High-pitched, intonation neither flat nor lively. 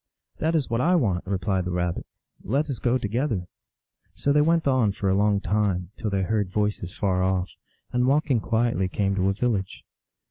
No: low, 105 Hz; average, 4.8 semitones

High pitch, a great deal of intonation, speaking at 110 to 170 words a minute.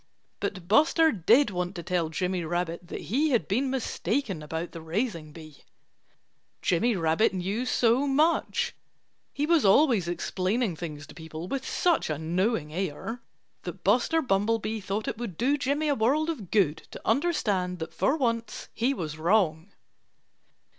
Yes: high, 200 Hz; wide, 7.0 semitones; average, 155 wpm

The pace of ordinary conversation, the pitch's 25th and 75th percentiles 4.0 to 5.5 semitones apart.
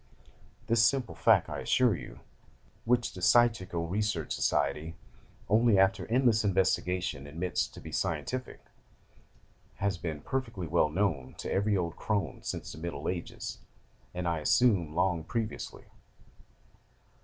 No: slow, 130 wpm; average, 5.1 semitones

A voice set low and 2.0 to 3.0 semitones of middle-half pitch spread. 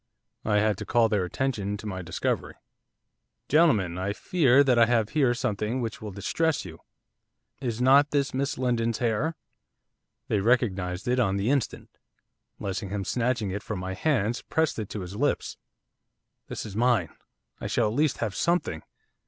No: low, 115 Hz; average, 4.5 semitones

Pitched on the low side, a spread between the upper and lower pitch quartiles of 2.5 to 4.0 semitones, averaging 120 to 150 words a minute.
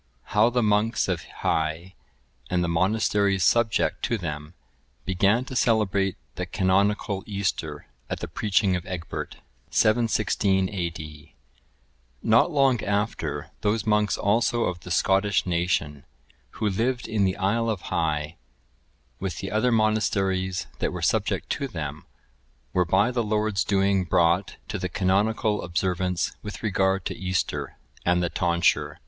Yes: very low, 95 Hz; average, 3.3 semitones; average, 140 wpm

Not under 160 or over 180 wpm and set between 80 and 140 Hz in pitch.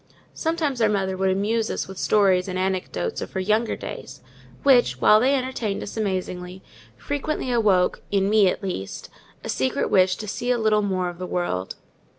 No: average, 170 wpm; high, 200 Hz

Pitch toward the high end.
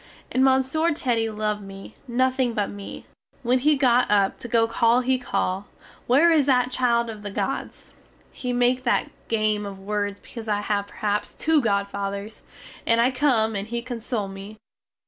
Yes: high, 230 Hz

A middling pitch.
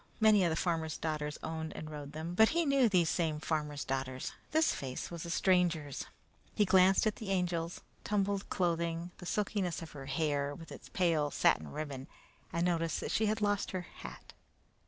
Yes: medium, 170 Hz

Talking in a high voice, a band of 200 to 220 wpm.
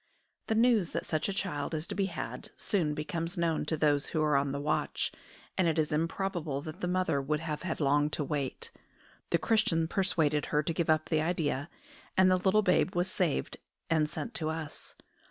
No: medium, 160 Hz; fast, 205 wpm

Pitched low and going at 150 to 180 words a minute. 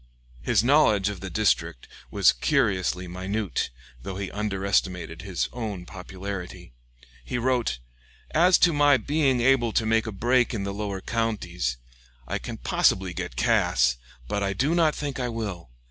Yes: low, 100 Hz; average, 155 wpm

